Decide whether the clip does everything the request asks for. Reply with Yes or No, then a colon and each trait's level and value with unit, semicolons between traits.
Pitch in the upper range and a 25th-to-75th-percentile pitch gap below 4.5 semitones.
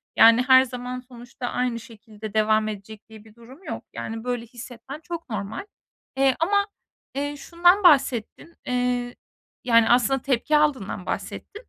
Yes: high, 245 Hz; average, 3.6 semitones